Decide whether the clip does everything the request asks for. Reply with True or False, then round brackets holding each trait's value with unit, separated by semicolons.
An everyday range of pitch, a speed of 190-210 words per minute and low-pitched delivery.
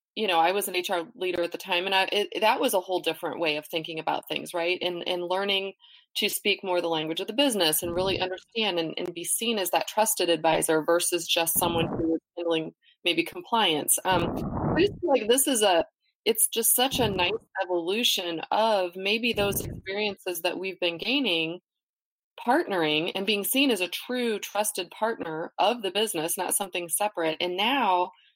False (3.9 semitones; 195 wpm; 185 Hz)